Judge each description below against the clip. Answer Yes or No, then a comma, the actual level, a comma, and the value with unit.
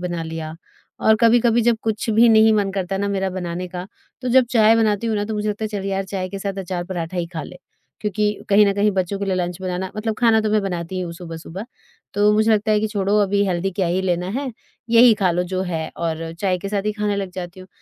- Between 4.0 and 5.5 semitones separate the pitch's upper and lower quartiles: No, average, 2.9 semitones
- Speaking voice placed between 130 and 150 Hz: No, high, 195 Hz